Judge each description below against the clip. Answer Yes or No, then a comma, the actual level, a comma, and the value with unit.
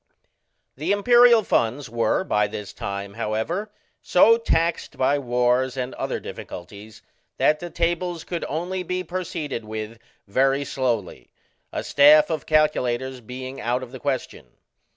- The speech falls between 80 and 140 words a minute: Yes, slow, 135 wpm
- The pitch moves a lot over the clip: Yes, wide, 6.4 semitones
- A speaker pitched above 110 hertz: Yes, low, 135 Hz